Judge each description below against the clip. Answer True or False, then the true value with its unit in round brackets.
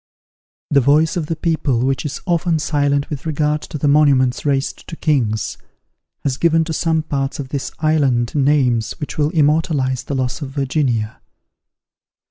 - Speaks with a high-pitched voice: False (145 Hz)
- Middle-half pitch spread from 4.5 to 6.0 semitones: False (2.7 semitones)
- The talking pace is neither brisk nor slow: True (160 wpm)